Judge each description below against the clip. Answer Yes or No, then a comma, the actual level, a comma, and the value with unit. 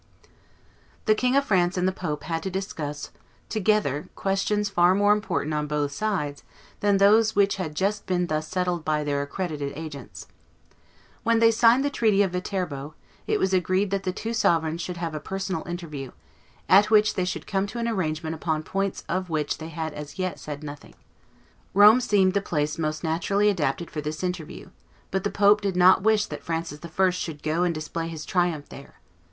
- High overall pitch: No, medium, 180 Hz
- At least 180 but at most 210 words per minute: Yes, average, 190 wpm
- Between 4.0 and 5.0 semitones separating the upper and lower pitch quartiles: Yes, average, 4.4 semitones